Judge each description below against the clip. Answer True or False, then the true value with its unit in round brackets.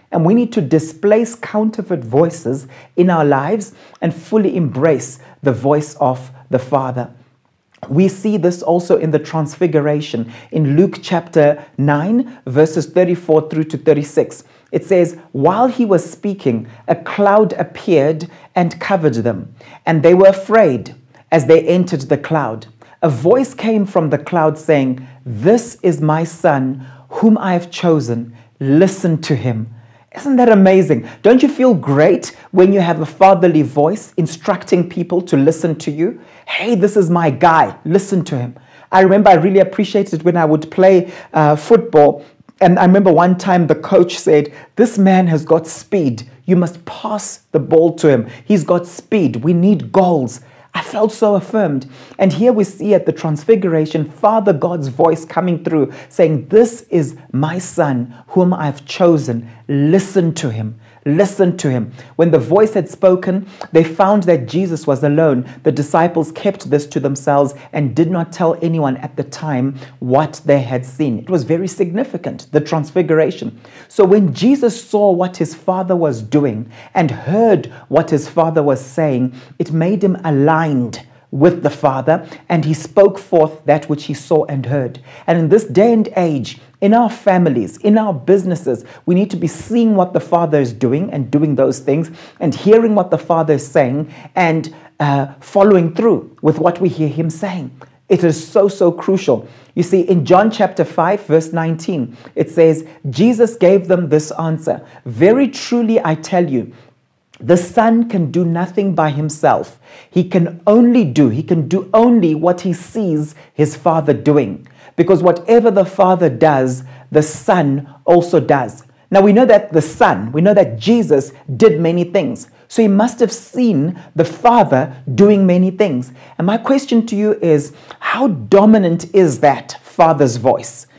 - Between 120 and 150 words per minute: False (170 wpm)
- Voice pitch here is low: False (165 Hz)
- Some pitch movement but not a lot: True (4.5 semitones)